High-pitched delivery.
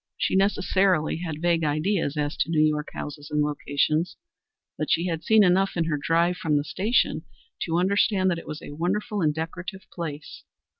No: medium, 165 Hz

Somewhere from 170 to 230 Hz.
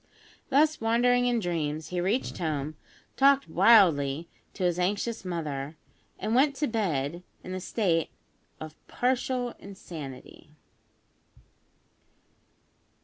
Yes: medium, 185 Hz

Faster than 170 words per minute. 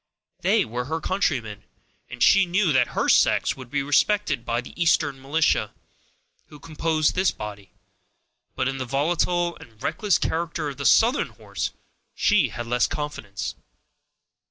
No: average, 150 wpm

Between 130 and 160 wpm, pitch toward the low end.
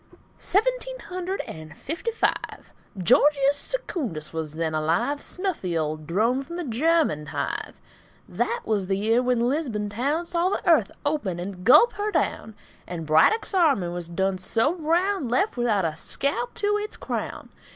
No: average, 155 wpm; very high, 250 Hz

